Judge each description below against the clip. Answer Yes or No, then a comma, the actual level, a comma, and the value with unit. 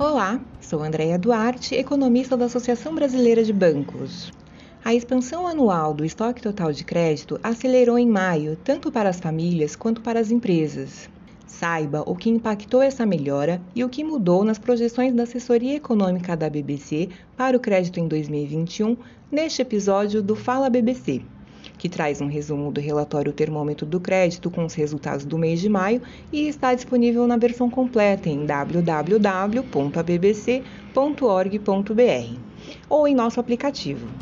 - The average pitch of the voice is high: Yes, high, 205 Hz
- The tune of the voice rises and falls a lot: Yes, wide, 7.7 semitones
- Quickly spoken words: No, average, 145 wpm